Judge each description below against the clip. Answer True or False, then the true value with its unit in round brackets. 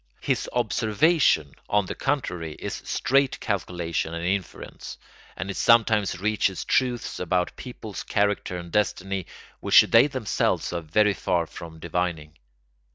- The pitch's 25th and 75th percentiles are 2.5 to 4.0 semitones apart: False (4.5 semitones)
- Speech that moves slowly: True (130 wpm)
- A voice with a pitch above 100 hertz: False (95 Hz)